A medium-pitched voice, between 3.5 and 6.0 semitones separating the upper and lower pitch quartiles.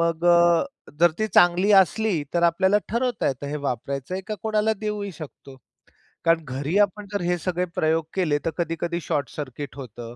Yes: medium, 170 Hz; average, 4.7 semitones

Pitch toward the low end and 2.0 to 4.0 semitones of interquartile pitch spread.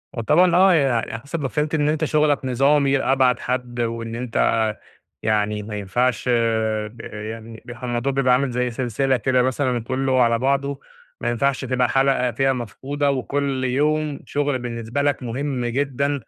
Yes: low, 130 Hz; average, 3.0 semitones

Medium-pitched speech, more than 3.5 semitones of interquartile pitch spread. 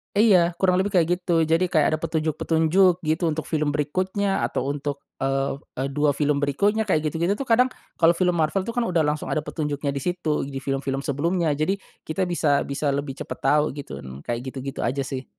Yes: medium, 155 Hz; average, 4.0 semitones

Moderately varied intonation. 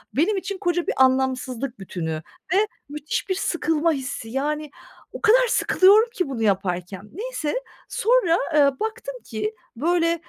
No: wide, 7.3 semitones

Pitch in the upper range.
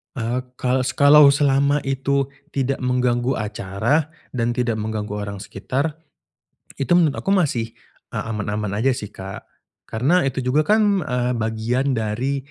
No: low, 125 Hz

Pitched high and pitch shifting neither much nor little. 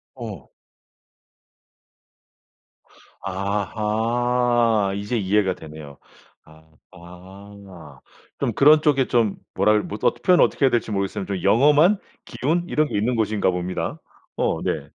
No: low, 105 Hz; average, 4.1 semitones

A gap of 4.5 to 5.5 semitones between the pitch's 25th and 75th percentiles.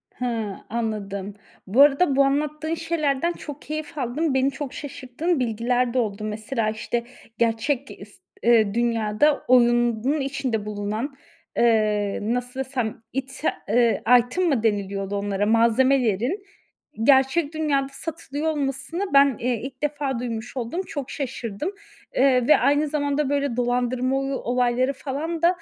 No: average, 3.9 semitones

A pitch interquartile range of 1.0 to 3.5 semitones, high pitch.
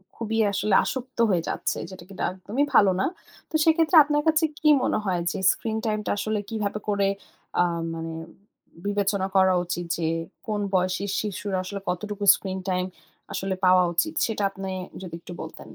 Yes: average, 2.9 semitones; high, 200 Hz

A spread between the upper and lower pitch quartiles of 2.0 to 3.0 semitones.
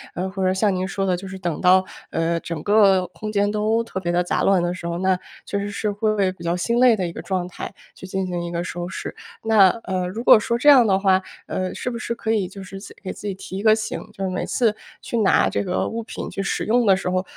Yes: average, 2.7 semitones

